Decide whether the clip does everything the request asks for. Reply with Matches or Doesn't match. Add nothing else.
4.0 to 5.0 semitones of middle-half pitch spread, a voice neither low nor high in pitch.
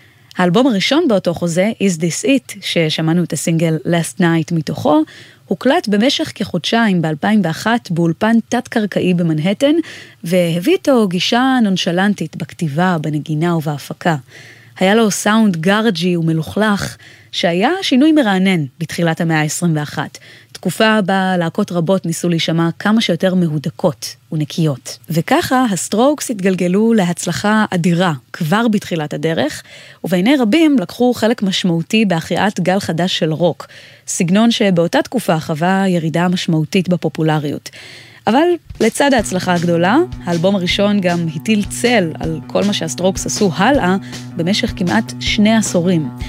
Matches